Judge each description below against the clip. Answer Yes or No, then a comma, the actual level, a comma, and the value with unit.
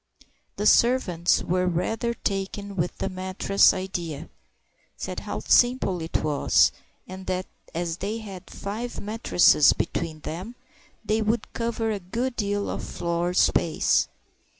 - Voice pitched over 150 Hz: Yes, high, 190 Hz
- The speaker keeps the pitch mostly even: No, average, 3.9 semitones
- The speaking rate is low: Yes, slow, 130 wpm